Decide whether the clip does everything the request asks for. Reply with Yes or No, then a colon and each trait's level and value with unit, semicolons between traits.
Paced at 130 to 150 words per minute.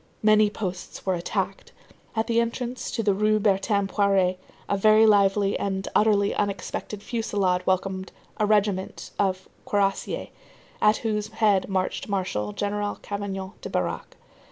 Yes: slow, 135 wpm